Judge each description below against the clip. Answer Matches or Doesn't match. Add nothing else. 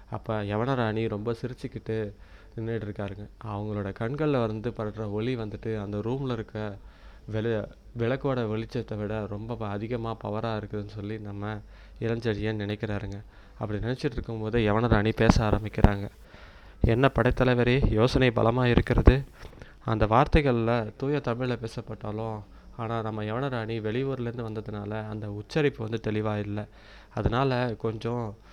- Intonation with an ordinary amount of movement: Doesn't match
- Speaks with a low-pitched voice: Matches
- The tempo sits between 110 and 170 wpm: Matches